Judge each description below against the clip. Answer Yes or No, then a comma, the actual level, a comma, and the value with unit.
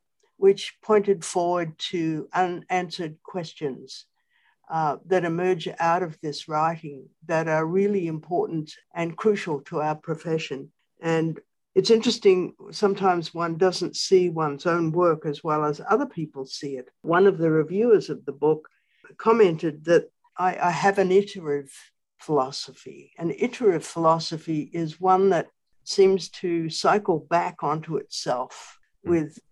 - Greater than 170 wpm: No, slow, 135 wpm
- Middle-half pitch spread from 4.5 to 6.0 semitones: No, average, 3.2 semitones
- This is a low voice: No, medium, 170 Hz